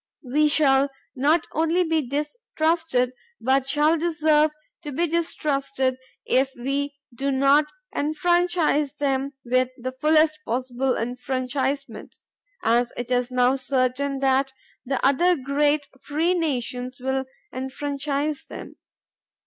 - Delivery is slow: Yes, slow, 115 wpm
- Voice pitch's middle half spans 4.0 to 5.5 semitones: No, average, 2.8 semitones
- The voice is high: Yes, very high, 275 Hz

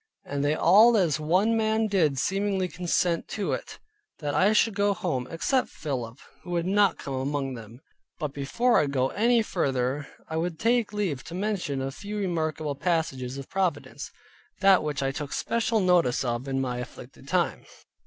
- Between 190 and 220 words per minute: No, average, 175 wpm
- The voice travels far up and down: Yes, wide, 6.6 semitones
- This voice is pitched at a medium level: Yes, medium, 165 Hz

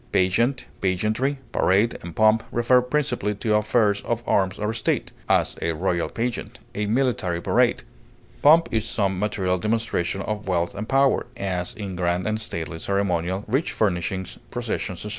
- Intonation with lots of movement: No, average, 3.8 semitones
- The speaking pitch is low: Yes, low, 105 Hz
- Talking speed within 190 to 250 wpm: No, average, 155 wpm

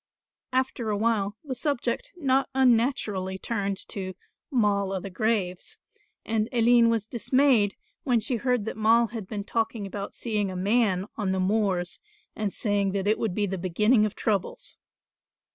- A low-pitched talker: No, high, 215 Hz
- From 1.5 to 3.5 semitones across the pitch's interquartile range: Yes, average, 3.2 semitones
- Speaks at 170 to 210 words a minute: No, average, 160 wpm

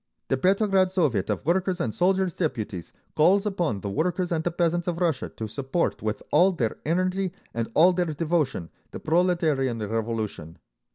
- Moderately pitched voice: Yes, medium, 165 Hz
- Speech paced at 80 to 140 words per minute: No, average, 165 wpm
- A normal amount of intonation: No, wide, 7.6 semitones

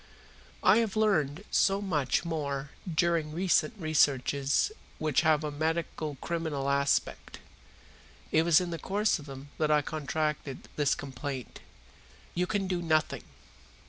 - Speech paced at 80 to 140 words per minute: Yes, slow, 135 wpm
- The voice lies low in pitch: No, medium, 155 Hz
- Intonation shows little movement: No, average, 3.3 semitones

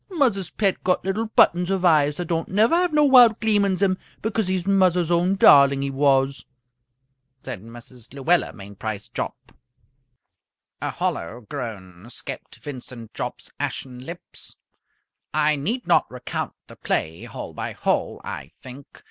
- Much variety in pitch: Yes, wide, 7.4 semitones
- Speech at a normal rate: Yes, average, 150 wpm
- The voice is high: No, medium, 165 Hz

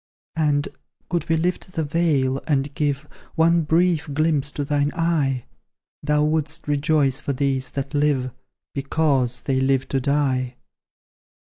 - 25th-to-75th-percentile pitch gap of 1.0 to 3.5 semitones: Yes, average, 2.7 semitones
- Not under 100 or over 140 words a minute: Yes, slow, 135 wpm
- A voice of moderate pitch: Yes, medium, 145 Hz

